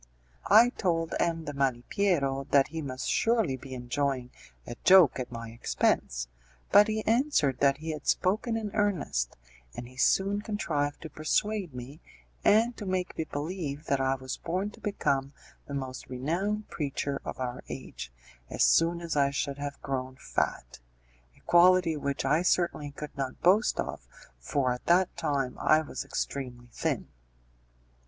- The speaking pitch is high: No, medium, 145 Hz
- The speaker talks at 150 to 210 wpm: Yes, average, 160 wpm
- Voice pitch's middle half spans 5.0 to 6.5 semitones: Yes, wide, 5.5 semitones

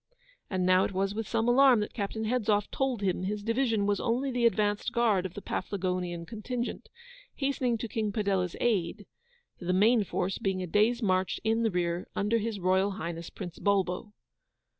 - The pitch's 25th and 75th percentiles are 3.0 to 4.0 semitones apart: Yes, average, 3.6 semitones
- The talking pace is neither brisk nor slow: Yes, average, 180 wpm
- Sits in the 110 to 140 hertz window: No, high, 205 Hz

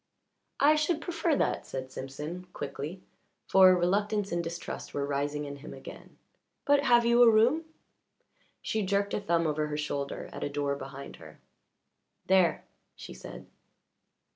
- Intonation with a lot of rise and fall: Yes, wide, 7.1 semitones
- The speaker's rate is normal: Yes, average, 150 wpm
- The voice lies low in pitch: No, medium, 175 Hz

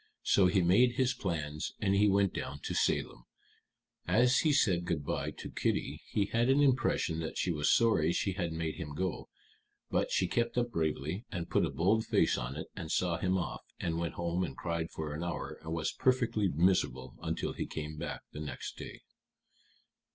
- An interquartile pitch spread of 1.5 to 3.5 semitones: No, average, 4.6 semitones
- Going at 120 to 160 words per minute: No, average, 195 wpm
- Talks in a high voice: No, very low, 85 Hz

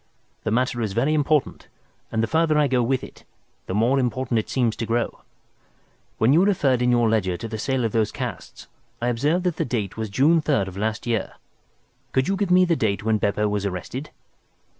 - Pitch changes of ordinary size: Yes, average, 4.6 semitones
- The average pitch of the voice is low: Yes, low, 120 Hz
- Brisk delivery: Yes, fast, 210 wpm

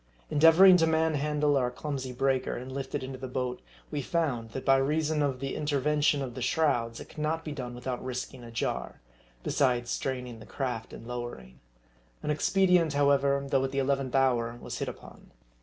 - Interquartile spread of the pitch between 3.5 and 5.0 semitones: No, average, 3.1 semitones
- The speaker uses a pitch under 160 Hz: Yes, low, 135 Hz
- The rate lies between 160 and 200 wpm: Yes, average, 190 wpm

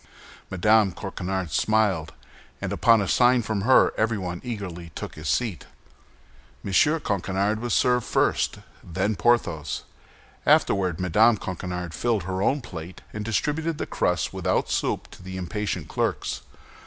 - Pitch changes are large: No, average, 4.1 semitones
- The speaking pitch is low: Yes, low, 100 Hz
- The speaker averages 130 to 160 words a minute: Yes, slow, 135 wpm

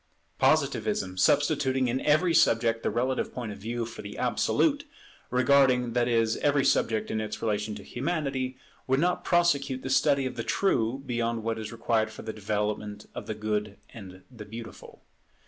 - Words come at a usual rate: Yes, average, 170 wpm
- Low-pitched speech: Yes, low, 120 Hz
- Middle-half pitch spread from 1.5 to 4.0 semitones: Yes, average, 3.5 semitones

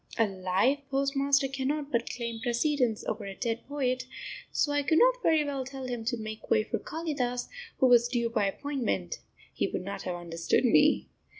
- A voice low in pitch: No, very high, 250 Hz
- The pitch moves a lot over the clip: No, average, 3.9 semitones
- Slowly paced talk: No, average, 185 wpm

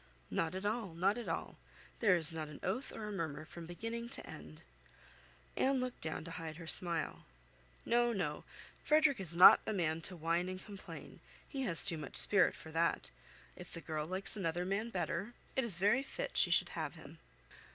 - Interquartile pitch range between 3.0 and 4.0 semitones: No, average, 4.8 semitones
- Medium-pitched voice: Yes, medium, 180 Hz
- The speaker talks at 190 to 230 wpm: Yes, average, 195 wpm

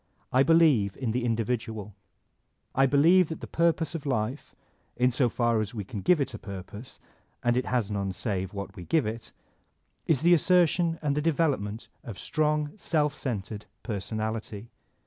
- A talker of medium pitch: No, low, 125 Hz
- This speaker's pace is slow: No, average, 165 wpm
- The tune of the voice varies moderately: No, wide, 6.0 semitones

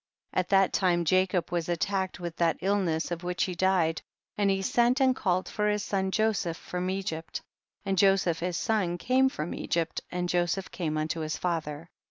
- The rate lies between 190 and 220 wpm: Yes, average, 195 wpm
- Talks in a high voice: No, medium, 180 Hz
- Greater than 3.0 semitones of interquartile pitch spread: No, narrow, 2.4 semitones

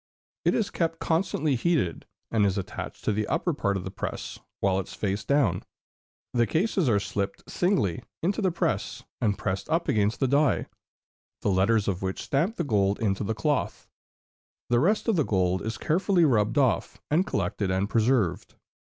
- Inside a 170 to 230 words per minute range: Yes, average, 175 wpm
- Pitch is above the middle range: No, low, 115 Hz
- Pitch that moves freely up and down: Yes, wide, 8.2 semitones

